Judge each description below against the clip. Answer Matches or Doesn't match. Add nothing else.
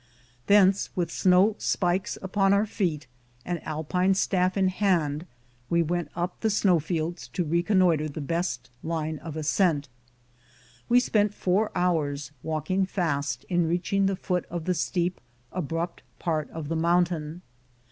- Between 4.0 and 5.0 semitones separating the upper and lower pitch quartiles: Doesn't match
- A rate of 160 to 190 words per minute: Doesn't match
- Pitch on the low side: Doesn't match